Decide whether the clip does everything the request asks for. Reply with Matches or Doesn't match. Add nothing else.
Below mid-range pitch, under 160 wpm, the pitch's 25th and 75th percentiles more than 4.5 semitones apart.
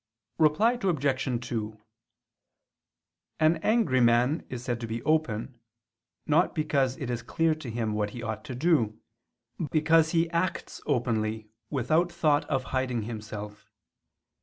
Matches